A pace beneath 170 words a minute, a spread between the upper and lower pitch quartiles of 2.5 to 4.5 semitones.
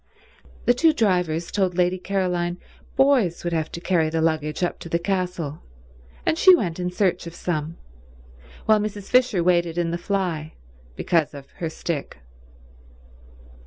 Yes: average, 155 wpm; average, 2.8 semitones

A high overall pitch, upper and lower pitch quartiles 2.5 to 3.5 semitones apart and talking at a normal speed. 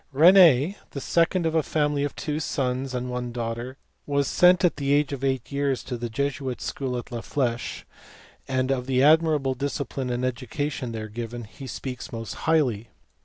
No: low, 135 Hz; average, 3.0 semitones; average, 180 wpm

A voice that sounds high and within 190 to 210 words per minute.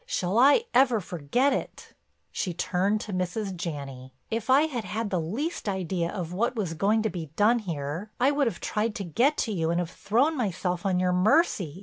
Yes: high, 195 Hz; fast, 205 wpm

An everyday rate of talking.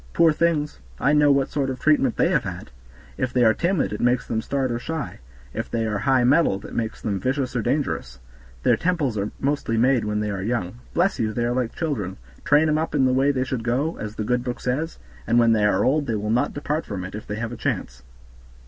No: fast, 245 wpm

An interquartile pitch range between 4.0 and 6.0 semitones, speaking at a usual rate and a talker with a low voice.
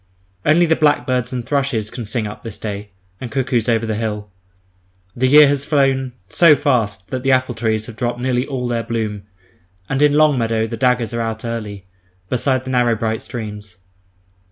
No: average, 3.2 semitones; average, 185 wpm; low, 120 Hz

